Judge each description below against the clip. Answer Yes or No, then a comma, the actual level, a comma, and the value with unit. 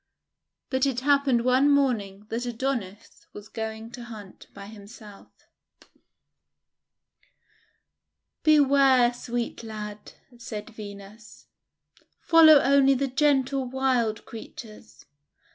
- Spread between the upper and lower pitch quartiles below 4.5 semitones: Yes, average, 4.0 semitones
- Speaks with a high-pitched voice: Yes, high, 240 Hz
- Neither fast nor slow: No, slow, 95 wpm